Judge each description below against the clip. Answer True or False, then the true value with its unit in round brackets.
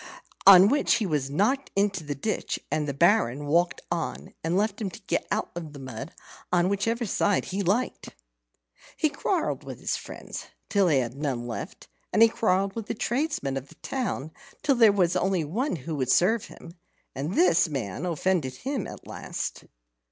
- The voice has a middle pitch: True (180 Hz)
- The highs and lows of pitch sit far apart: True (6.5 semitones)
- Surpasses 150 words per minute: True (185 wpm)